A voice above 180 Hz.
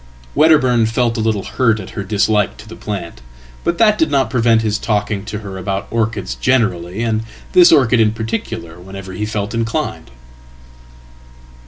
No: low, 110 Hz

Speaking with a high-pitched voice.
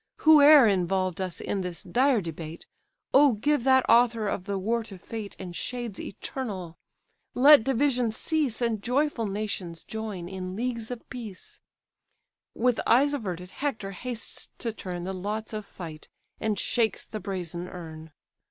Yes: high, 215 Hz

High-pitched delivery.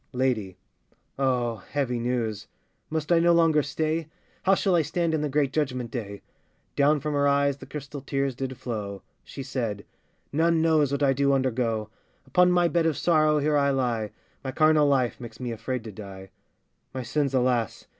No: low, 135 Hz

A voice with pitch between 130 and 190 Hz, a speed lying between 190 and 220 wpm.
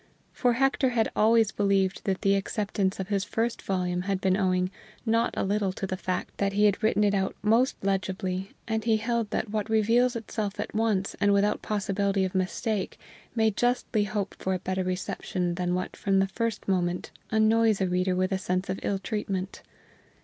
No: high, 200 Hz; average, 195 wpm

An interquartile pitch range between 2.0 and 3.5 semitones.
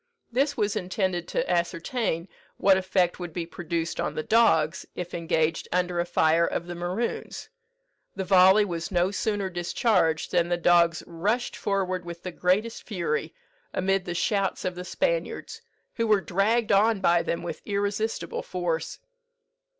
Yes: average, 2.9 semitones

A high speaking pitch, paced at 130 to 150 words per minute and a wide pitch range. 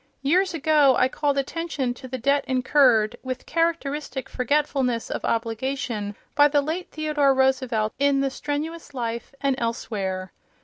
No: very high, 270 Hz; average, 140 wpm; average, 3.4 semitones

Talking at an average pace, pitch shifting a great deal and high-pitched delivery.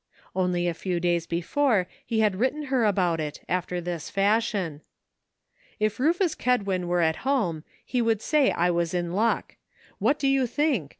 Yes: average, 175 wpm; wide, 6.3 semitones; high, 195 Hz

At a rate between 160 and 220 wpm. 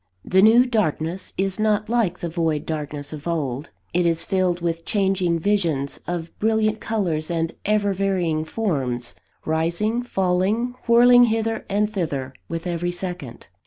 No: average, 145 wpm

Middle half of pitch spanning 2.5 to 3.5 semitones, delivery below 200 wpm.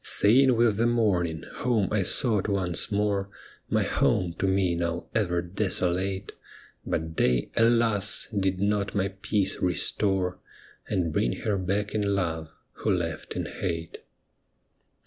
Yes: average, 3.2 semitones; average, 140 wpm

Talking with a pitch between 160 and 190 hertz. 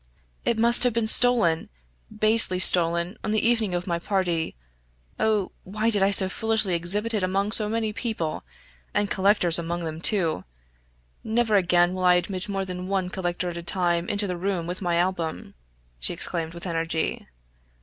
Yes: medium, 185 Hz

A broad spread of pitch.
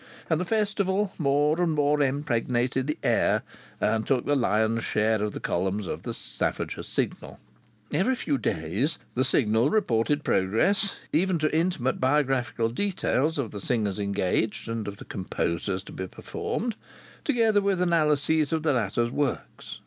Yes: wide, 6.5 semitones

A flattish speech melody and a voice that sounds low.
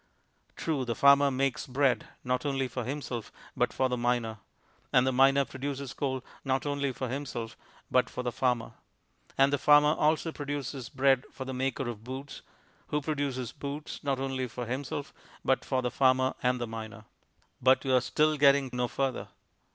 Yes: narrow, 2.0 semitones; low, 130 Hz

